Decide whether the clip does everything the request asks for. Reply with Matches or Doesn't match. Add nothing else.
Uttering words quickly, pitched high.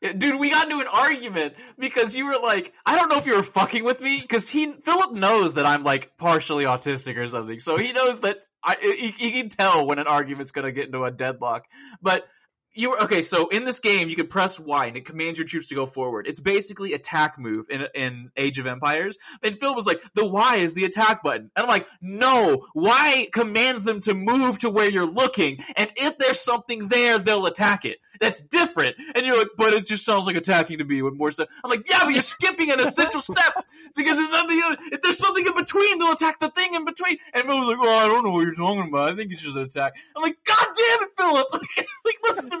Matches